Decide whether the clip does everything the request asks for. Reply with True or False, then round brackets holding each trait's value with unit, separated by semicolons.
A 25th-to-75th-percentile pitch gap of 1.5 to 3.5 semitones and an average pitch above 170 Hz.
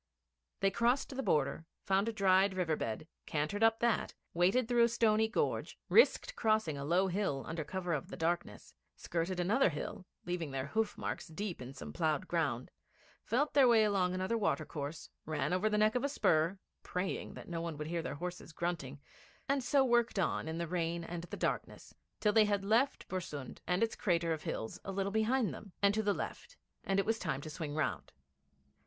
False (5.1 semitones; 185 Hz)